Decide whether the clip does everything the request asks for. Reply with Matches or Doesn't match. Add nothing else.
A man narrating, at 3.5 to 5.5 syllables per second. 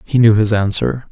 Matches